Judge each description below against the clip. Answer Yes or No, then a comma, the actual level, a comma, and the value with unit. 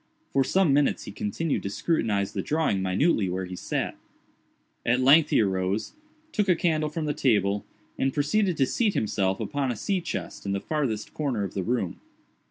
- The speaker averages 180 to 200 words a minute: Yes, average, 185 wpm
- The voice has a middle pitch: No, low, 130 Hz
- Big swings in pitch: Yes, wide, 7.7 semitones